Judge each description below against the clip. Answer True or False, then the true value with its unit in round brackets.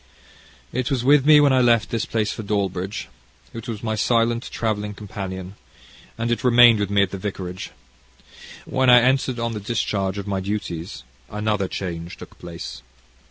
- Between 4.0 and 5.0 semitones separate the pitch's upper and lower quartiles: False (3.4 semitones)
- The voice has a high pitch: False (105 Hz)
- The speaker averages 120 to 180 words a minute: True (170 wpm)